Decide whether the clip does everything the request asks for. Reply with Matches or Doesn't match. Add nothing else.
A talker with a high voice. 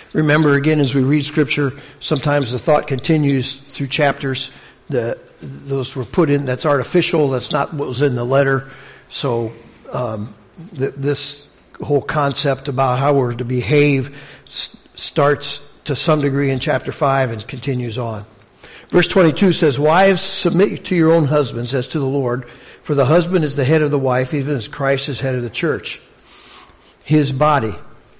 Doesn't match